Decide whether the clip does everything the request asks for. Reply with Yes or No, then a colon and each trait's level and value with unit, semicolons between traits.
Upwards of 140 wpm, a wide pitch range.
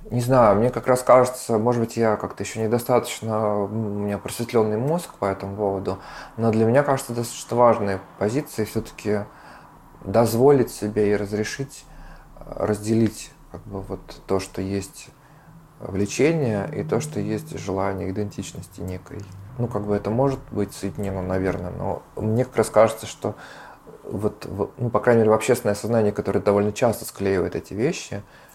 No: average, 155 wpm; average, 3.4 semitones